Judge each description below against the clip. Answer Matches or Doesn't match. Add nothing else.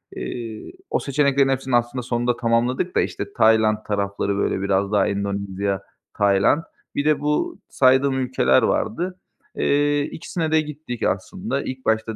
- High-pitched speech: Doesn't match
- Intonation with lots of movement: Matches